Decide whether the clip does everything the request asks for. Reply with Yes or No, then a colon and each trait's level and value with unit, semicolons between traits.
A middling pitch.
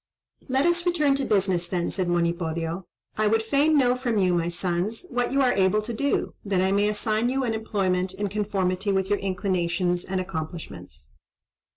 No: high, 195 Hz